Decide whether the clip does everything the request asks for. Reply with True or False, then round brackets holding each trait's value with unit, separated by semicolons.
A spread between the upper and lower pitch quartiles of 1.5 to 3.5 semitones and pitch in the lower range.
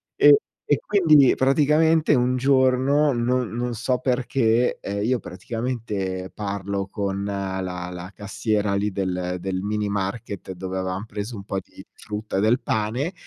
False (4.6 semitones; 105 Hz)